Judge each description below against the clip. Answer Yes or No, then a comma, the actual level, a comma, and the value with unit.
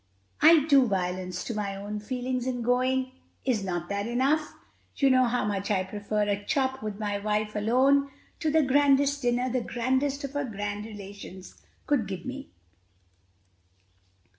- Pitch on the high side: Yes, high, 240 Hz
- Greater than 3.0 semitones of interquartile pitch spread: Yes, average, 4.6 semitones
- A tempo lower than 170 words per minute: Yes, average, 160 wpm